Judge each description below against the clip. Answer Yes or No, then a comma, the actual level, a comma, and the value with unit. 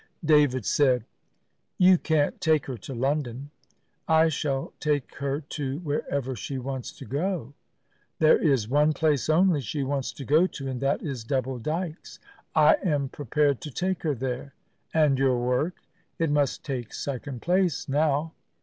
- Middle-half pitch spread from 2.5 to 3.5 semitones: Yes, average, 2.8 semitones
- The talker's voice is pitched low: No, medium, 145 Hz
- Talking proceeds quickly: No, average, 160 wpm